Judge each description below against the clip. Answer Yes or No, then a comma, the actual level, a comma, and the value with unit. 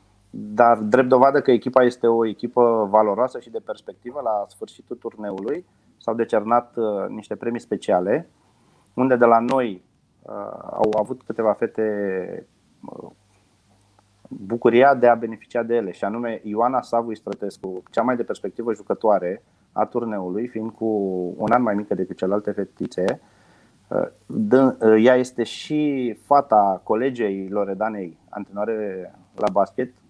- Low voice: Yes, low, 110 Hz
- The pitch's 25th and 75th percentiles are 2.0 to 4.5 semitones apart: Yes, average, 2.8 semitones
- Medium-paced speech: Yes, average, 130 wpm